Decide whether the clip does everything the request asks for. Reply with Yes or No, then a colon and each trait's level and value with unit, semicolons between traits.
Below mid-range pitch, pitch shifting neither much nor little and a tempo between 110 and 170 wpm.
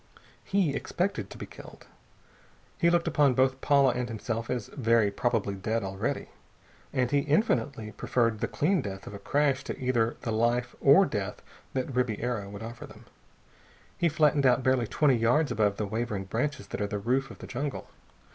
No: low, 125 Hz; average, 4.0 semitones; average, 180 wpm